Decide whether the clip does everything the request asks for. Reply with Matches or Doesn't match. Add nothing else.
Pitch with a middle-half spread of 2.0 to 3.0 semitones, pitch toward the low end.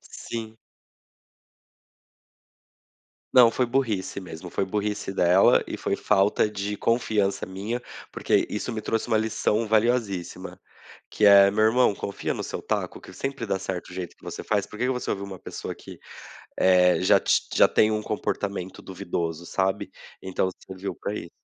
Matches